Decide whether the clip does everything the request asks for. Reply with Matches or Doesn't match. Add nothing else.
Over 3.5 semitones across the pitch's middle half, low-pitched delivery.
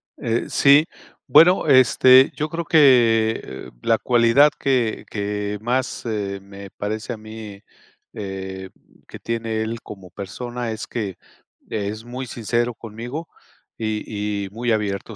Doesn't match